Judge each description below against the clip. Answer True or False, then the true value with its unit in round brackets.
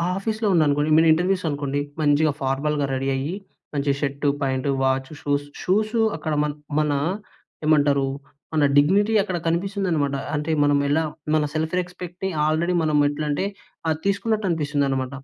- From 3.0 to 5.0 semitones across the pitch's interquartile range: True (3.9 semitones)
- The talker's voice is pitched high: False (150 Hz)